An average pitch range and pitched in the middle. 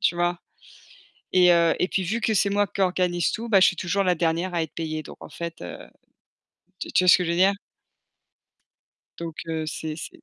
No: narrow, 2.3 semitones; medium, 175 Hz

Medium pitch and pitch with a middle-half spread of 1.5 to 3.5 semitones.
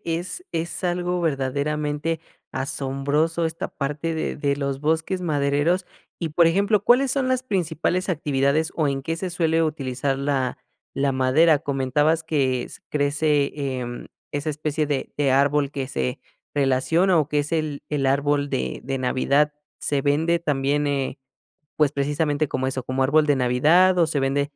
Yes: medium, 145 Hz; average, 2.9 semitones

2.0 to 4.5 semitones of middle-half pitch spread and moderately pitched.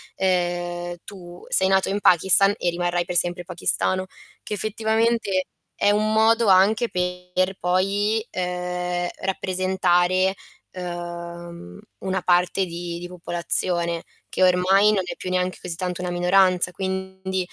No: narrow, 1.5 semitones; medium, 180 Hz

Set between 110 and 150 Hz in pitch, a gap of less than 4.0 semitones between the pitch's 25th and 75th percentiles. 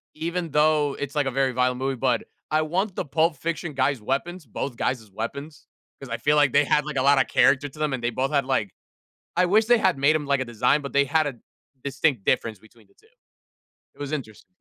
Yes: medium, 140 Hz; average, 3.0 semitones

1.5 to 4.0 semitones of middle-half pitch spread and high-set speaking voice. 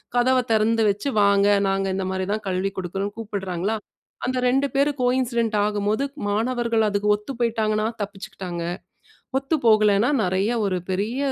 Yes: average, 3.0 semitones; high, 210 Hz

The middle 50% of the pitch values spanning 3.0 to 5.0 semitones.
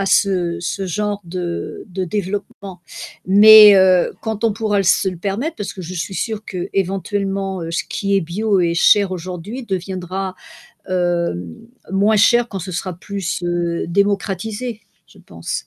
No: narrow, 2.6 semitones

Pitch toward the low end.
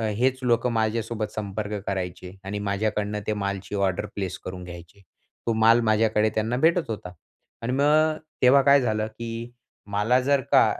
Yes: low, 110 Hz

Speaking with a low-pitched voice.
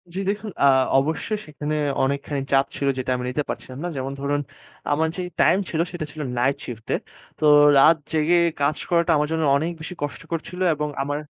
No: medium, 150 Hz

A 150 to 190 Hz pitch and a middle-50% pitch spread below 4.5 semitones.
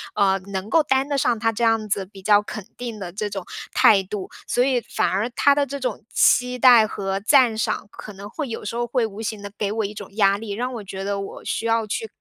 No: high, 220 Hz; average, 3.3 semitones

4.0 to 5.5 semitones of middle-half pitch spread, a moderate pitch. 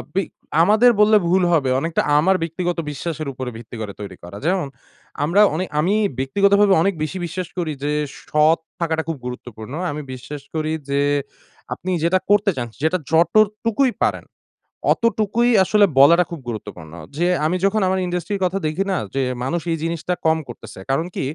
Yes: average, 4.8 semitones; medium, 170 Hz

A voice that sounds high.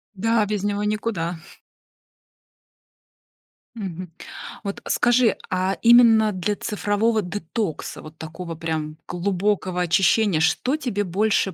Yes: high, 200 Hz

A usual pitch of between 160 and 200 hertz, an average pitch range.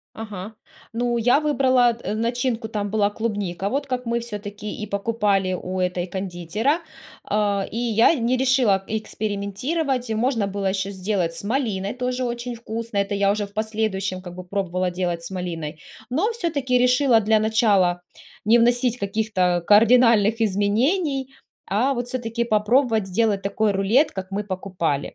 No: high, 215 Hz; average, 3.7 semitones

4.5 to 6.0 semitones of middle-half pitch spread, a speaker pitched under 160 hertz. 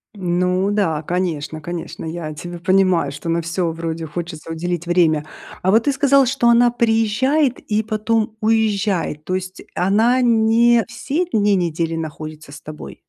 No: average, 5.3 semitones; medium, 185 Hz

